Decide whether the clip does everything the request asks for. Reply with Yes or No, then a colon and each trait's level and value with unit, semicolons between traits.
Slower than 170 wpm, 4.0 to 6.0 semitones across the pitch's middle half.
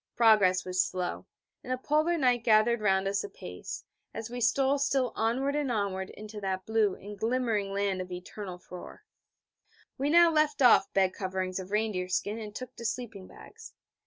No: average, 175 wpm; average, 4.9 semitones